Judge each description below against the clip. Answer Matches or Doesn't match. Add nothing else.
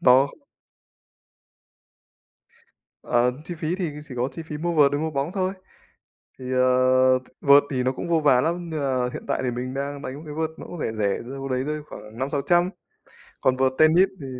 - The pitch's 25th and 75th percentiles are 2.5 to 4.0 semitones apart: Matches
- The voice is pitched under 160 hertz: Matches